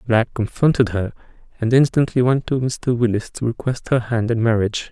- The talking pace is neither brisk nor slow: Yes, average, 195 wpm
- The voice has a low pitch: Yes, low, 120 Hz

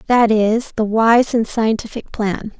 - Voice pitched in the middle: No, high, 225 Hz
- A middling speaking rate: Yes, average, 160 wpm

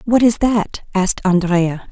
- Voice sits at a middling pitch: No, high, 200 Hz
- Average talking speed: Yes, average, 155 wpm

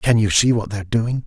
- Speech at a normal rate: No, fast, 330 wpm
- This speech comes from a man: Yes, male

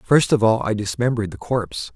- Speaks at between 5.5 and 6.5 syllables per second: Yes, 6.2 syllables/s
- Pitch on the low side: Yes, low, 110 Hz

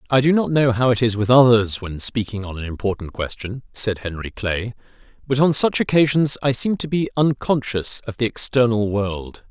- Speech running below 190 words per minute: No, average, 195 wpm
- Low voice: Yes, low, 120 Hz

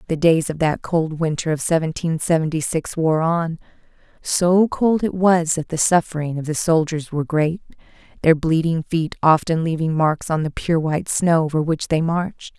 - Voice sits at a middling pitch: Yes, medium, 165 Hz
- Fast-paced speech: No, average, 185 wpm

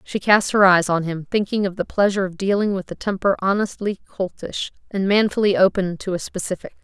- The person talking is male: No, female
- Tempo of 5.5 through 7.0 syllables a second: Yes, 5.7 syllables/s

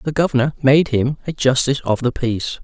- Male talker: Yes, male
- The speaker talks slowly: No, fast, 205 wpm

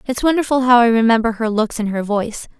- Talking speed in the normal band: No, fast, 230 wpm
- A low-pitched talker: No, high, 230 Hz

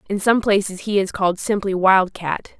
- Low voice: No, high, 195 Hz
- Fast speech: Yes, fast, 210 wpm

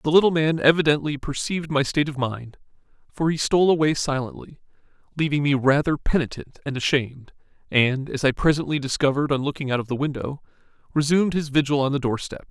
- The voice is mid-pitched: Yes, medium, 145 Hz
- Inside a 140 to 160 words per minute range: No, average, 175 wpm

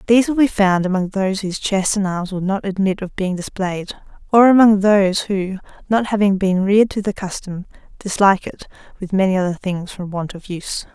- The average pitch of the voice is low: No, high, 195 Hz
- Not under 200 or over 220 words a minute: Yes, fast, 205 wpm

